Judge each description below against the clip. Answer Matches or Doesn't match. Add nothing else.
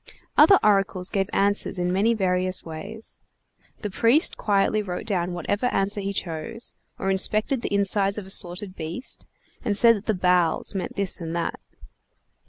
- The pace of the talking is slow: Doesn't match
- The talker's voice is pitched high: Matches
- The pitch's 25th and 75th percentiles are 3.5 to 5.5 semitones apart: Doesn't match